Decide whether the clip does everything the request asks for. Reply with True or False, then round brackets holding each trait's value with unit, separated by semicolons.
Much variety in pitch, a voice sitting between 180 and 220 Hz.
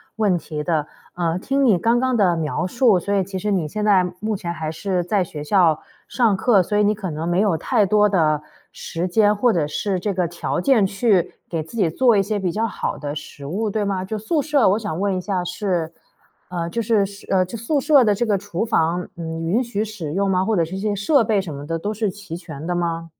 False (3.9 semitones; 195 Hz)